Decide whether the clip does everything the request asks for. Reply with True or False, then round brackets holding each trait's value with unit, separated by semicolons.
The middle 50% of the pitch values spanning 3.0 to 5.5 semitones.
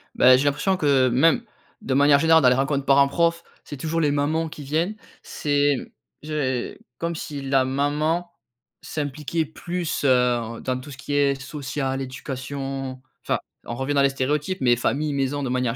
False (2.5 semitones)